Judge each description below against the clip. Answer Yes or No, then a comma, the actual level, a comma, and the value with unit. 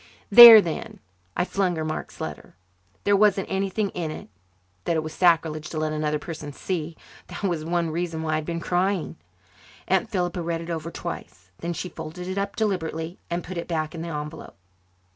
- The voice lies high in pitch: No, medium, 170 Hz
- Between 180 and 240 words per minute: Yes, average, 195 wpm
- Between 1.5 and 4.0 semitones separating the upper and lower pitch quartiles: Yes, narrow, 2.6 semitones